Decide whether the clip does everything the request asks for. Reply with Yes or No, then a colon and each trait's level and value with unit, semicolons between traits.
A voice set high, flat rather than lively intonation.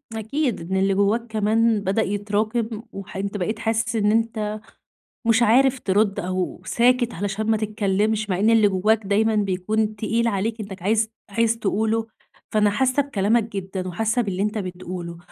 Yes: high, 215 Hz; narrow, 2.3 semitones